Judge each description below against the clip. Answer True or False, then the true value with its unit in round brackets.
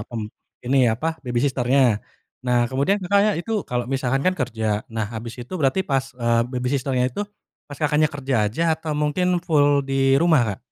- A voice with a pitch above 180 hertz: False (135 Hz)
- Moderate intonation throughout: True (3.9 semitones)